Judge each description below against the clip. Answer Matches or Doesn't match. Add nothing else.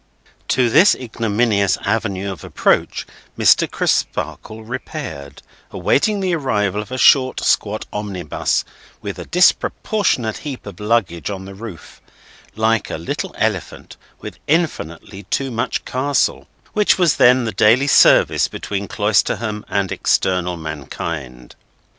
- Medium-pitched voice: Doesn't match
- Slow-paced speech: Matches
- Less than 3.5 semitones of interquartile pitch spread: Doesn't match